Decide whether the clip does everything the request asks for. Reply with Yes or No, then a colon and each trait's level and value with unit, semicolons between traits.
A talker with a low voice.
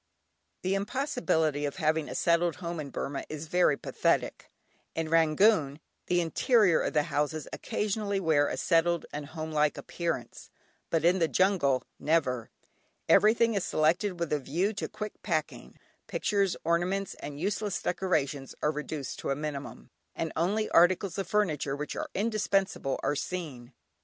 No: medium, 165 Hz